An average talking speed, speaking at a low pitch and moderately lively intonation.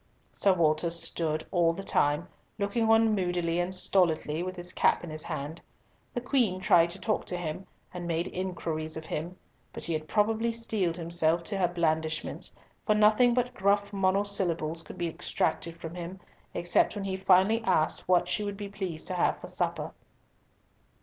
No: average, 175 wpm; medium, 180 Hz; average, 3.3 semitones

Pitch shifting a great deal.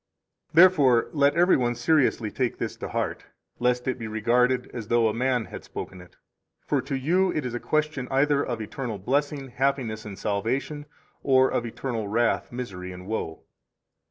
No: average, 3.8 semitones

